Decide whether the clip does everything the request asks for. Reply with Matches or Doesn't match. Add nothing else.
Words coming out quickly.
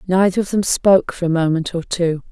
Matches